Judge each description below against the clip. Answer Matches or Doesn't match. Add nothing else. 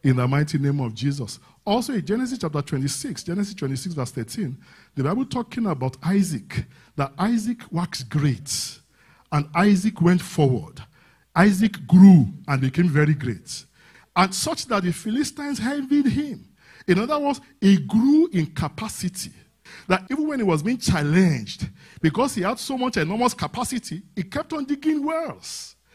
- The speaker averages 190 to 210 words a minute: Doesn't match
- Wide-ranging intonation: Matches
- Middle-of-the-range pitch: Matches